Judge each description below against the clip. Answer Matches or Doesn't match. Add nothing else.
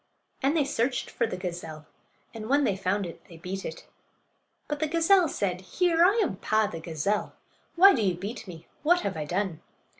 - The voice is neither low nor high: Doesn't match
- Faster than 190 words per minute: Matches